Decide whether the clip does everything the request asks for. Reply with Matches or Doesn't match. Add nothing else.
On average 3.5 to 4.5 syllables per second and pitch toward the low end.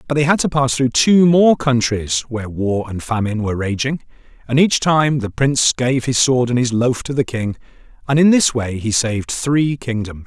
Doesn't match